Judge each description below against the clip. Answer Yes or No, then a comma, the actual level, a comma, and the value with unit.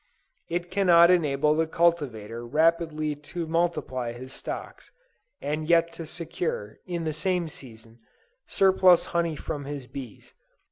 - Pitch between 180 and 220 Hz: No, medium, 160 Hz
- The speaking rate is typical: No, slow, 125 wpm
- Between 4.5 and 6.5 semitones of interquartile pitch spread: No, average, 3.8 semitones